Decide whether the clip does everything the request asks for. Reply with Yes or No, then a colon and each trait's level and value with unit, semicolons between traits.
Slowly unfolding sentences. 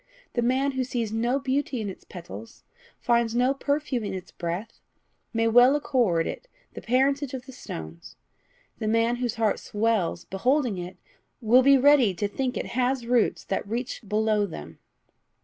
No: average, 165 wpm